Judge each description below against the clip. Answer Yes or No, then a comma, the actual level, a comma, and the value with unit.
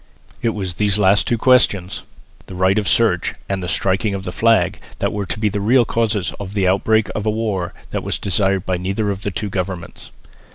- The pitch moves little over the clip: Yes, narrow, 2.3 semitones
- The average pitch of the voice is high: No, low, 100 Hz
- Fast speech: Yes, fast, 215 wpm